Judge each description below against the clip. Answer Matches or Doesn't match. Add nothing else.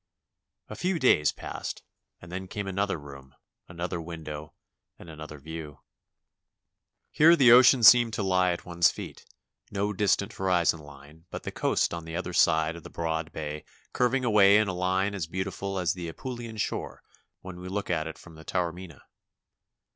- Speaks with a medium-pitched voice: Doesn't match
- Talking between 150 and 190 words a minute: Matches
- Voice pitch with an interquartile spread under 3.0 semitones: Doesn't match